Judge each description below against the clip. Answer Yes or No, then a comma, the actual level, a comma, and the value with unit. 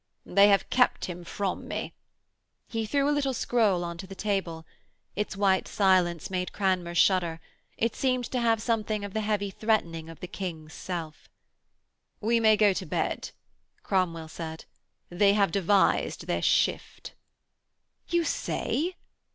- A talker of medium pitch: No, high, 195 Hz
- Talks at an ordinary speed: Yes, average, 150 wpm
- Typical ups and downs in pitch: Yes, average, 3.8 semitones